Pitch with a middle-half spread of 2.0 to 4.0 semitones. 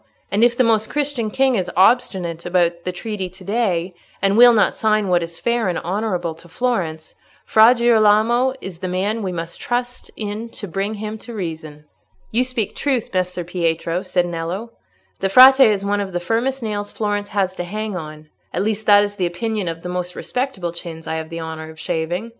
No: average, 4.4 semitones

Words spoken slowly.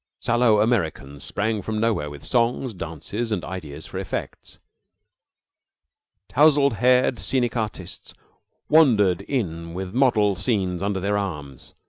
Yes: slow, 120 wpm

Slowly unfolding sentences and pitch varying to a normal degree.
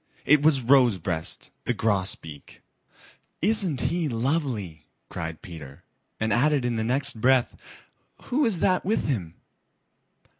No: slow, 120 wpm; wide, 8.1 semitones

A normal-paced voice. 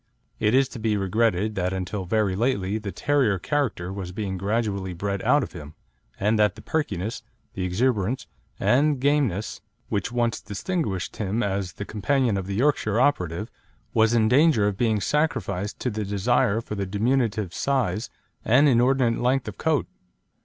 Yes: average, 160 wpm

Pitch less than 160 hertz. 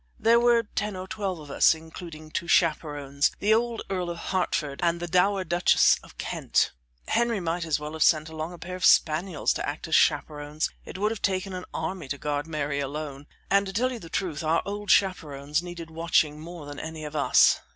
No: medium, 170 Hz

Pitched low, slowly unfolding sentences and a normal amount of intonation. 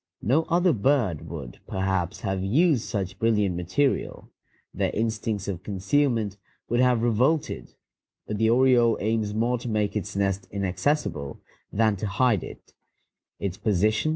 Yes: low, 110 Hz; slow, 130 wpm; average, 4.2 semitones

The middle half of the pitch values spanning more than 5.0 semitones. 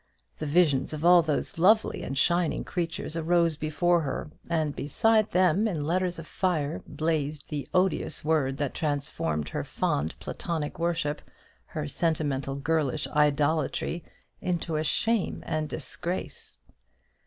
No: average, 2.9 semitones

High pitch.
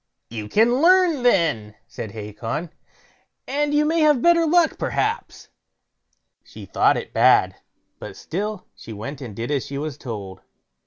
No: medium, 170 Hz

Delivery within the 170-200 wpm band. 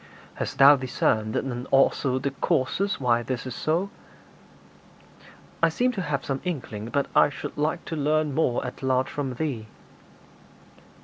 No: average, 145 wpm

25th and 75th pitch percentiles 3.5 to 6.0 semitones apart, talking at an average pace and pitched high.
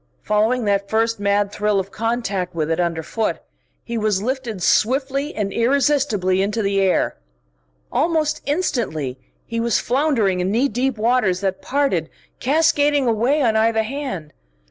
Yes: average, 5.1 semitones; average, 145 wpm; high, 225 Hz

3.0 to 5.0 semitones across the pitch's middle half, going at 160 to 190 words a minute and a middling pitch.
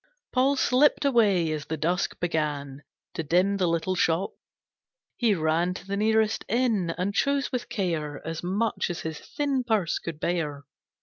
No: wide, 5.4 semitones; average, 165 wpm; medium, 180 Hz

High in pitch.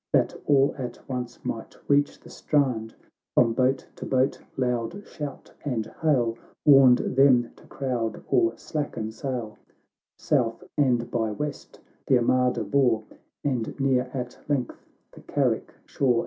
No: low, 125 Hz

